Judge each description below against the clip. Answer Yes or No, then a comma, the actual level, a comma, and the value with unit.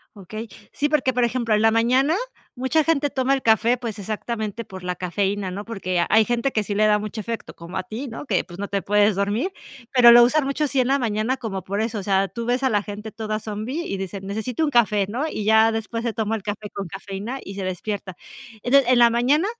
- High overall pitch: Yes, high, 220 Hz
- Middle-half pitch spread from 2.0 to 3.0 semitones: No, average, 3.5 semitones